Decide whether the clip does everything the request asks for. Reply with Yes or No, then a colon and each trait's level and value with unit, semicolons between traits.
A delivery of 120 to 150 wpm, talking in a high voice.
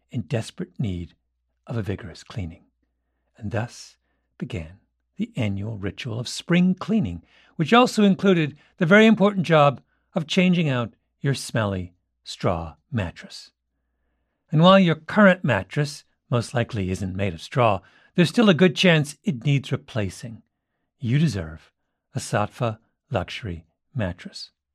No: slow, 135 wpm; low, 120 Hz